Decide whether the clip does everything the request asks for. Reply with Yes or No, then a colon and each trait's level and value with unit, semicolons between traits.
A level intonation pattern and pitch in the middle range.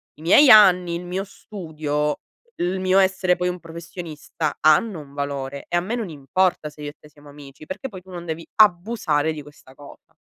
No: average, 4.0 semitones; medium, 170 Hz